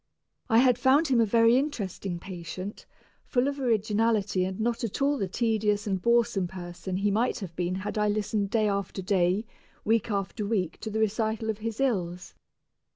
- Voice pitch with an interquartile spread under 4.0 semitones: Yes, average, 3.3 semitones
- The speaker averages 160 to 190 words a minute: Yes, average, 180 wpm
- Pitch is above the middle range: Yes, high, 210 Hz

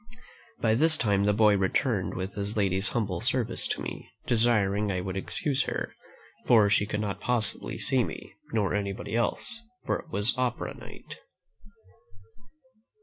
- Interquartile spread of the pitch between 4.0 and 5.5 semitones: No, average, 3.0 semitones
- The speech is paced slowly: No, average, 150 wpm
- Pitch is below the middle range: Yes, low, 105 Hz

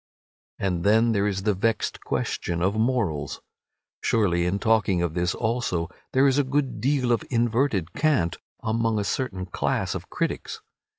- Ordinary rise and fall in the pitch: Yes, average, 5.0 semitones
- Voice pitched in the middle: No, low, 110 Hz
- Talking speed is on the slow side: No, average, 160 wpm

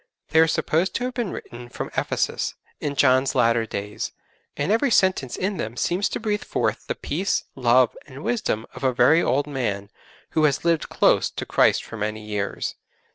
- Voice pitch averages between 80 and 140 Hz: Yes, low, 135 Hz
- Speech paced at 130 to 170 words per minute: No, average, 185 wpm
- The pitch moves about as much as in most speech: No, wide, 6.9 semitones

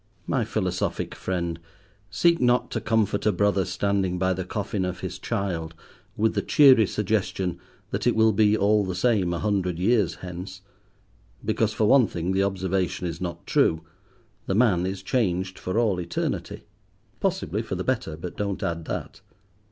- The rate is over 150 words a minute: Yes, average, 165 wpm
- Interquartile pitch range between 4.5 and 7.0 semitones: No, average, 3.0 semitones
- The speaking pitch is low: Yes, very low, 95 Hz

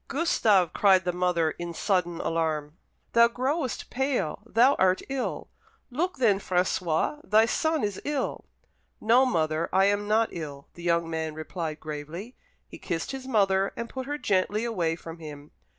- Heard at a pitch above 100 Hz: Yes, high, 190 Hz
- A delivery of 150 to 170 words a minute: Yes, average, 160 wpm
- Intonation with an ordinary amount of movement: No, wide, 6.2 semitones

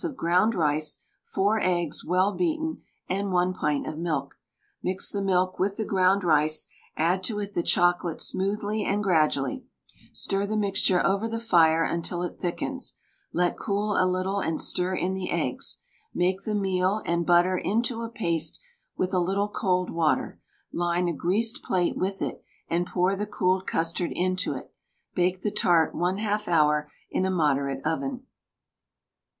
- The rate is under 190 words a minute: Yes, average, 165 wpm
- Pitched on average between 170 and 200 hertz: Yes, medium, 185 Hz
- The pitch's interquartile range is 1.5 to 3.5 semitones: Yes, average, 2.7 semitones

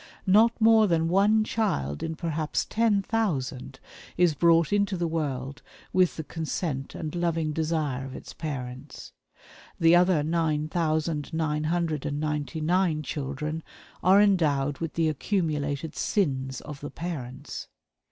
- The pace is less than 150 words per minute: Yes, average, 140 wpm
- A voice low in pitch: No, medium, 160 Hz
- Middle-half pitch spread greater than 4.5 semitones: No, average, 3.3 semitones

